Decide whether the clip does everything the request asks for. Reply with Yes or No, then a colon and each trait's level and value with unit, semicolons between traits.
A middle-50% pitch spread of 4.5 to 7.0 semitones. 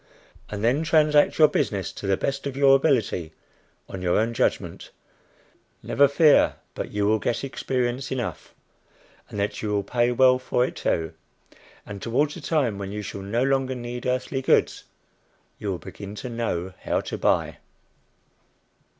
Yes: average, 4.9 semitones